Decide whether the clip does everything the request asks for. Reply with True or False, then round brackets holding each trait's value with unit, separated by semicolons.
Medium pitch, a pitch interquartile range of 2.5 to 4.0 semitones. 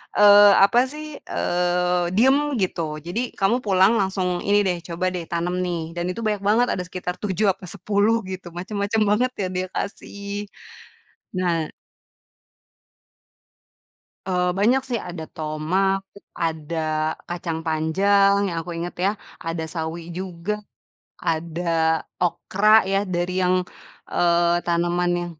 True (180 Hz; 2.8 semitones)